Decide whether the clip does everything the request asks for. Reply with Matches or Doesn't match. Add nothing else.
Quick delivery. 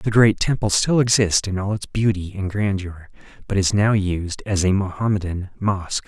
Doesn't match